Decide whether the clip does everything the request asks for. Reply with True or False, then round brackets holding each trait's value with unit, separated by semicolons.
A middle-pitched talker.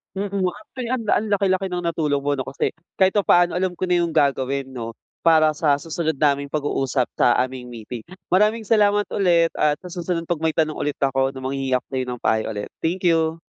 True (160 Hz)